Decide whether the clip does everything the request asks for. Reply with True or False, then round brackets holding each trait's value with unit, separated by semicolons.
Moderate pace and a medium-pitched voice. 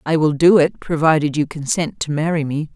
False (220 wpm; 155 Hz)